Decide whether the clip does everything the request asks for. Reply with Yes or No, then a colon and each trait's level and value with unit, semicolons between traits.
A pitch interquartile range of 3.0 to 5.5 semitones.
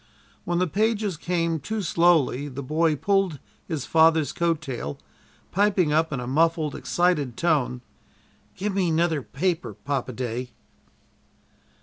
Yes: average, 4.0 semitones